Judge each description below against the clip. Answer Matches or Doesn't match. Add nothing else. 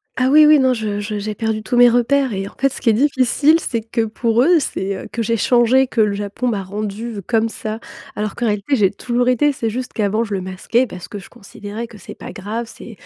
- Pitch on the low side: Doesn't match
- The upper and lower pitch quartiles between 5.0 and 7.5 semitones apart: Doesn't match